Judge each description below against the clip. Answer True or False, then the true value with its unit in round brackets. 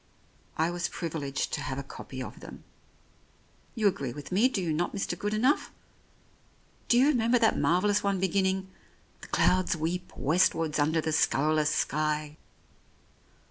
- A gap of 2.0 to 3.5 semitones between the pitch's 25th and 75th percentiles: False (4.6 semitones)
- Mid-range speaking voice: True (175 Hz)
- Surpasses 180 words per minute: False (155 wpm)